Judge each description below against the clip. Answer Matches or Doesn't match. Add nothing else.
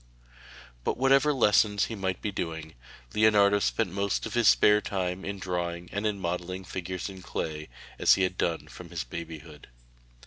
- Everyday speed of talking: Matches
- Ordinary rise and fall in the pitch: Matches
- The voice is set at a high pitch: Doesn't match